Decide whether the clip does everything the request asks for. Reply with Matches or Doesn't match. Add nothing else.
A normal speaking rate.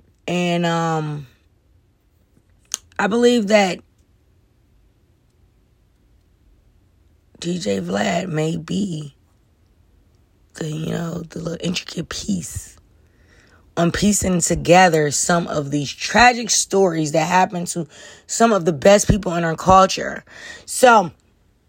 Doesn't match